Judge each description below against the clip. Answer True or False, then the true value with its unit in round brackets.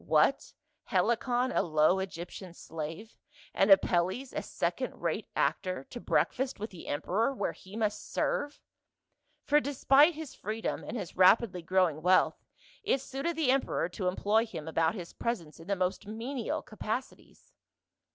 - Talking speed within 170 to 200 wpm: False (150 wpm)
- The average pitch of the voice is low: False (205 Hz)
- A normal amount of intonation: False (5.8 semitones)